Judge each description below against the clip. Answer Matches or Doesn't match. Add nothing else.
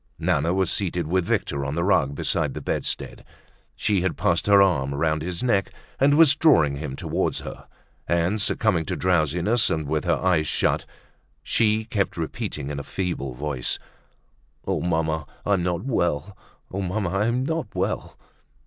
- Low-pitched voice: Matches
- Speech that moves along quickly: Doesn't match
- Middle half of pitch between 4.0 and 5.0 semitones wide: Matches